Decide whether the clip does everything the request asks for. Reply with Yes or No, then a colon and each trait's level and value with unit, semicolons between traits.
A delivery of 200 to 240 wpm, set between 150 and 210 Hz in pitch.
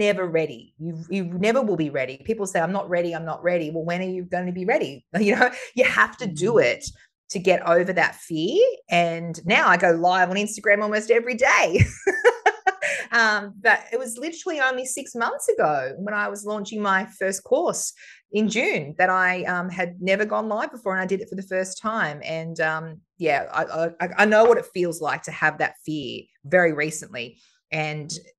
Yes: fast, 205 wpm; high, 190 Hz